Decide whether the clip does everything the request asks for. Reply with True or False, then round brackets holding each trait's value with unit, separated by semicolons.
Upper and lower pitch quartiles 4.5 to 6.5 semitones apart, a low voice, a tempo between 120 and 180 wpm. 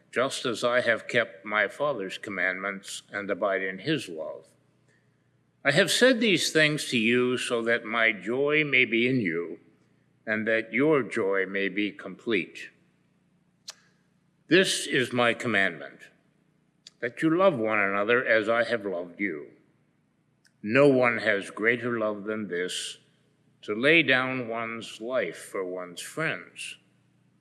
True (4.8 semitones; 115 Hz; 140 wpm)